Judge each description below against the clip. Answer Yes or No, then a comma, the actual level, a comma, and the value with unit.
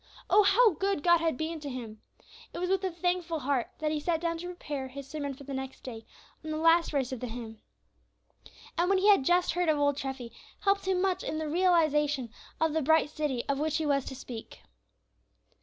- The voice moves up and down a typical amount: Yes, average, 4.4 semitones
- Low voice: No, very high, 310 Hz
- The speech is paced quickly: Yes, fast, 225 wpm